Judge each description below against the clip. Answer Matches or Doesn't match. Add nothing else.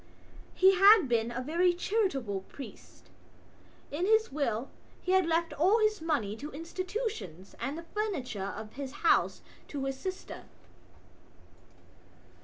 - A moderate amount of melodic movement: Doesn't match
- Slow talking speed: Matches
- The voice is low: Doesn't match